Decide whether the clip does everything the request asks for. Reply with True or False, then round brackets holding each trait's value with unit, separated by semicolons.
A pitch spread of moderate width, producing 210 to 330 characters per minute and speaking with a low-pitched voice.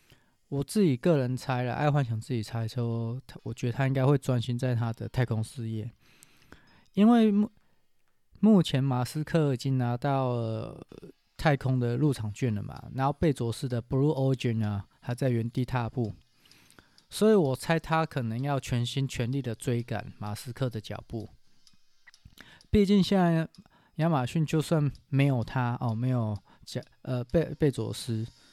True (4.0 semitones; 250 characters per minute; 130 Hz)